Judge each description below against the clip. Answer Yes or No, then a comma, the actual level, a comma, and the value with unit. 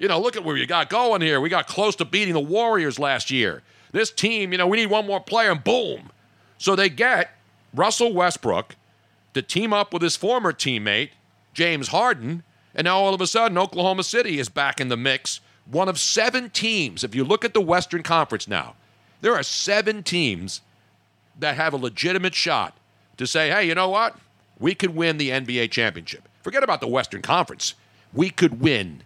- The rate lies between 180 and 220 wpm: Yes, average, 200 wpm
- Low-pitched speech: No, medium, 170 Hz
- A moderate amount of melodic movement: No, wide, 8.3 semitones